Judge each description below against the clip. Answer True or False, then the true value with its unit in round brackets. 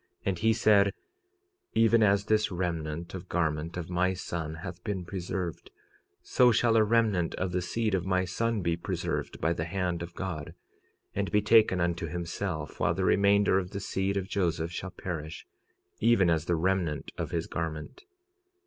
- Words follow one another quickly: False (170 wpm)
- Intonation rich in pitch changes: False (3.2 semitones)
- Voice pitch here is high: False (90 Hz)